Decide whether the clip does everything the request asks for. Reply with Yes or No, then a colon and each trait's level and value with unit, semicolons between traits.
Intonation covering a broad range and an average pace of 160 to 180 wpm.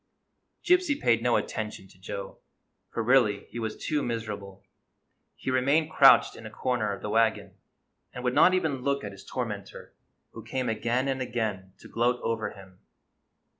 No: average, 3.7 semitones; average, 170 wpm